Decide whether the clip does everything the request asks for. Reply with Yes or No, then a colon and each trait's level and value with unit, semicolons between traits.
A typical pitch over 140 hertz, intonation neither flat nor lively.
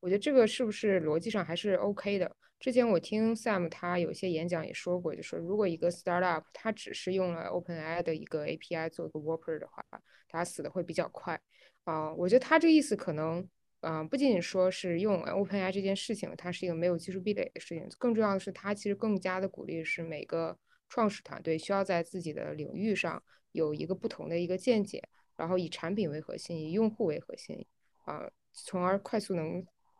Yes: medium, 185 Hz; average, 3.6 semitones